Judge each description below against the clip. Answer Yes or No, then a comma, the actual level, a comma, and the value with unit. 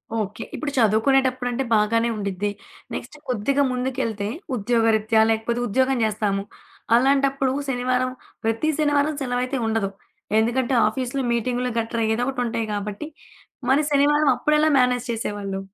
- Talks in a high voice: Yes, high, 245 Hz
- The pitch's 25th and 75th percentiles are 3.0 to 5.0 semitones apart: Yes, average, 3.4 semitones